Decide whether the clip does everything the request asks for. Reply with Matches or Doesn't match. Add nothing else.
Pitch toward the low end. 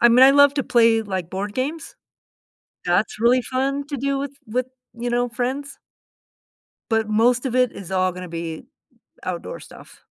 Doesn't match